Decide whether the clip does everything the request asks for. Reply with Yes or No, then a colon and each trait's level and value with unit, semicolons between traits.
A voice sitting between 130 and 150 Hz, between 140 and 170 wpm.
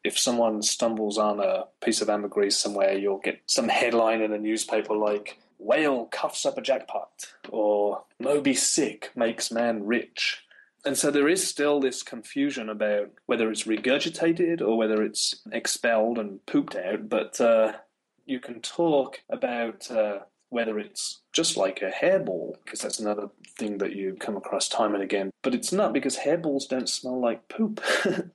No: low, 115 Hz; average, 165 wpm